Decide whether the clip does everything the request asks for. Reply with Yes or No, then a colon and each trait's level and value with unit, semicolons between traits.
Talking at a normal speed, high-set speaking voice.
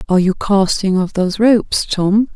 Yes: average, 180 wpm; high, 200 Hz